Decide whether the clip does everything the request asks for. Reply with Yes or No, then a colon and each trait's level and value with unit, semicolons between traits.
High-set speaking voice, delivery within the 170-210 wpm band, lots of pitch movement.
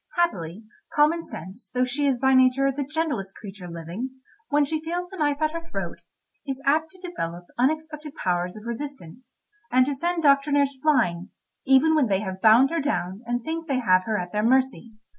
Yes: very high, 265 Hz; average, 190 wpm; wide, 6.4 semitones